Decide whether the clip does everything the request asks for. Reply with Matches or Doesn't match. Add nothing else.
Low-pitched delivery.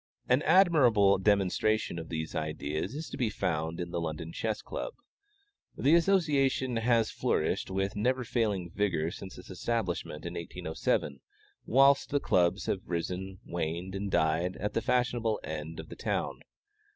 Matches